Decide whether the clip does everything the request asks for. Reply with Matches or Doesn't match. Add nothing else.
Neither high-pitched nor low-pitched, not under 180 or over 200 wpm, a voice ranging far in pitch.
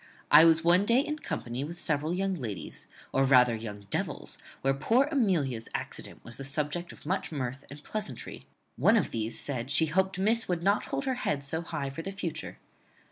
Matches